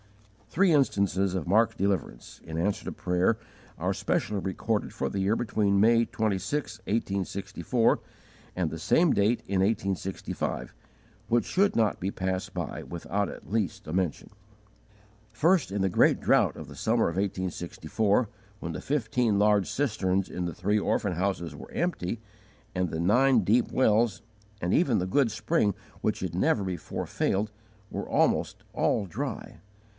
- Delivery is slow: No, average, 155 wpm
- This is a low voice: Yes, low, 100 Hz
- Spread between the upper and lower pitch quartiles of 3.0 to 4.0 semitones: Yes, average, 3.5 semitones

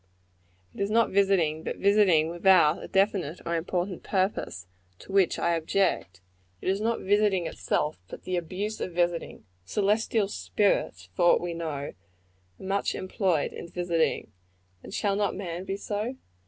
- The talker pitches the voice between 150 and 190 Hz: Yes, medium, 185 Hz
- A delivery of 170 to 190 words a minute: No, average, 155 wpm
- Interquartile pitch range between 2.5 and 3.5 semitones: Yes, average, 3.2 semitones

